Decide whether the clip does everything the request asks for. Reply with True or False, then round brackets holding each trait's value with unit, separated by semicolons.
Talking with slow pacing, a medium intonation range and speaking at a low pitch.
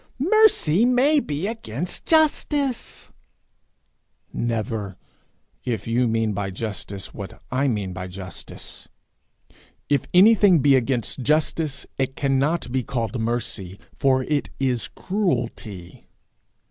False (110 wpm; 7.6 semitones; 130 Hz)